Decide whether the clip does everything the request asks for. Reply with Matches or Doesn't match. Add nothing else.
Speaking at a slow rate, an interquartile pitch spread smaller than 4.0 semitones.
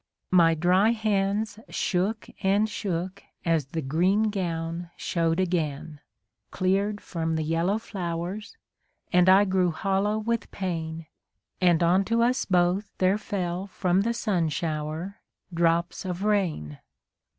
Matches